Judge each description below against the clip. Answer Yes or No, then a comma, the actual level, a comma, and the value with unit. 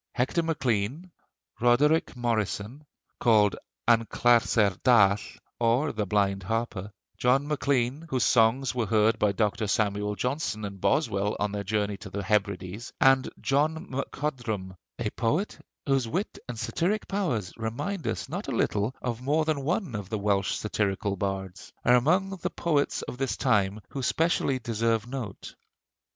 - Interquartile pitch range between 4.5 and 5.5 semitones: Yes, average, 4.9 semitones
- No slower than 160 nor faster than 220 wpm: No, average, 150 wpm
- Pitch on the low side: Yes, low, 115 Hz